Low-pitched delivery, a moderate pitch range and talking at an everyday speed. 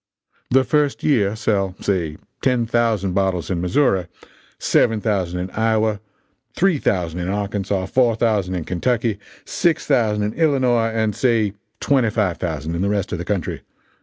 Yes: low, 105 Hz; average, 4.1 semitones; average, 160 wpm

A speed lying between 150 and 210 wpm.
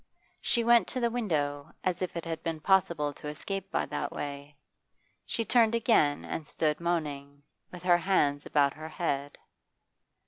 Yes: average, 165 wpm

